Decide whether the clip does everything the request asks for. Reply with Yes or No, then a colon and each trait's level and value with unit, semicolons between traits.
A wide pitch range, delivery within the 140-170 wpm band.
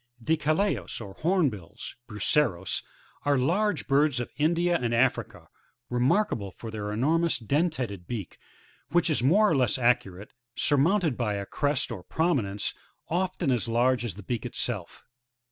Yes: wide, 6.7 semitones; average, 150 wpm